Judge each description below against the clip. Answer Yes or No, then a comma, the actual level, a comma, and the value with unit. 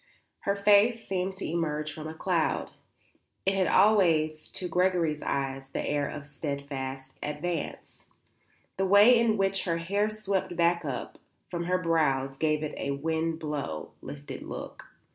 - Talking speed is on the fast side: No, average, 155 wpm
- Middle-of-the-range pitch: Yes, medium, 165 Hz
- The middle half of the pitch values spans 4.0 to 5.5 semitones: Yes, average, 4.5 semitones